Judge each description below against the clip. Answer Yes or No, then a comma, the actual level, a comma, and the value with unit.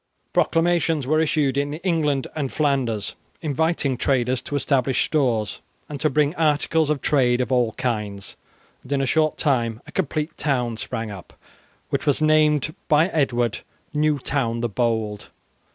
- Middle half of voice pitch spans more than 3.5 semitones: Yes, average, 4.0 semitones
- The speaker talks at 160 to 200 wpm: No, average, 150 wpm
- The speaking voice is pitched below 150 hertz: Yes, medium, 140 Hz